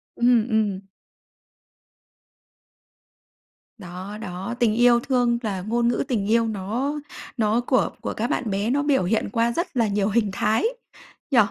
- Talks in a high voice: Yes, high, 230 Hz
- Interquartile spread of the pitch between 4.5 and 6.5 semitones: No, average, 2.8 semitones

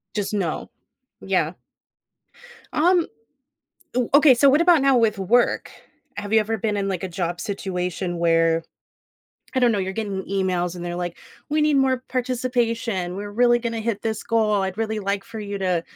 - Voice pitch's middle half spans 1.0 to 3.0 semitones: No, average, 4.3 semitones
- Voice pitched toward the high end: Yes, high, 210 Hz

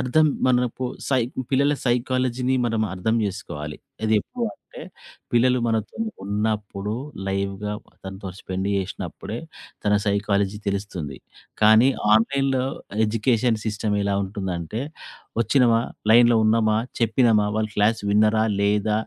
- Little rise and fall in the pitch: No, average, 3.1 semitones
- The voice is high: No, low, 110 Hz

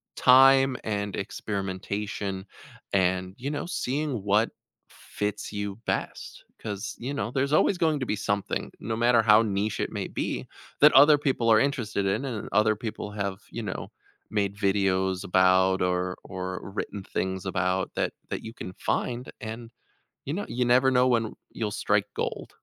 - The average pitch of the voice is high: No, low, 105 Hz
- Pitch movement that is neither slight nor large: Yes, average, 4.3 semitones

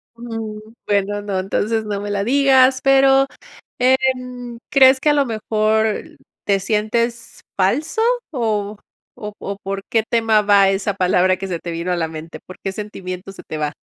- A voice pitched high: Yes, high, 210 Hz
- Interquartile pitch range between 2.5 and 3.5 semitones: No, average, 4.1 semitones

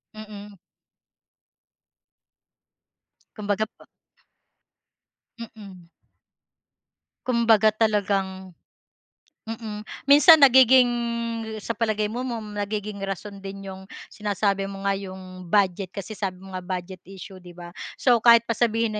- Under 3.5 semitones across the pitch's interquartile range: Yes, average, 2.7 semitones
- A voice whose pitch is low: No, high, 205 Hz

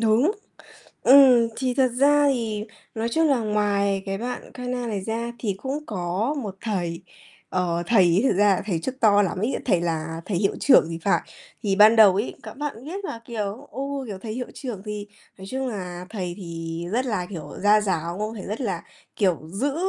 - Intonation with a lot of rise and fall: No, average, 4.8 semitones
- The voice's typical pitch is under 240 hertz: Yes, high, 210 Hz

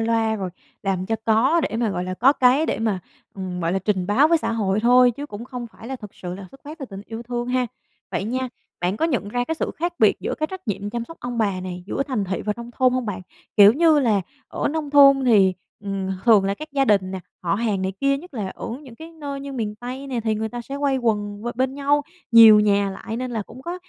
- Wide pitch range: No, average, 4.8 semitones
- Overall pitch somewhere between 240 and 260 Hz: No, high, 230 Hz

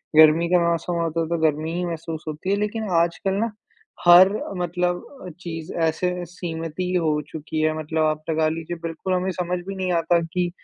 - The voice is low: No, medium, 170 Hz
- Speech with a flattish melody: Yes, narrow, 2.1 semitones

